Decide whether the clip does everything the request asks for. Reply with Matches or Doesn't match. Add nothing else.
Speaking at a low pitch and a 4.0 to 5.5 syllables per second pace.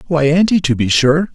Doesn't match